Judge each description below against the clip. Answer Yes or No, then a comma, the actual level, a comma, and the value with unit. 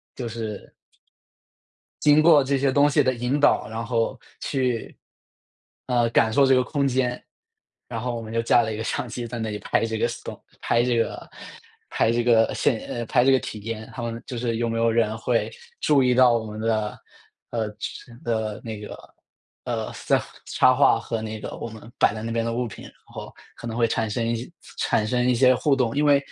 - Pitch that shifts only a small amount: Yes, narrow, 2.1 semitones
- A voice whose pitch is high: No, low, 115 Hz